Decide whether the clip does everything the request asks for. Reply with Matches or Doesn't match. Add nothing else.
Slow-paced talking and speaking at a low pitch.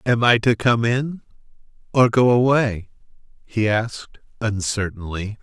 Matches